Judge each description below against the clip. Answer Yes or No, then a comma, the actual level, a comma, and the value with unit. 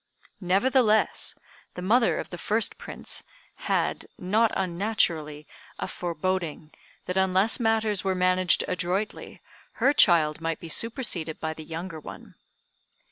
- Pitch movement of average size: Yes, average, 4.5 semitones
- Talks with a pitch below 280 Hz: Yes, medium, 185 Hz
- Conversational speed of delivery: No, slow, 125 wpm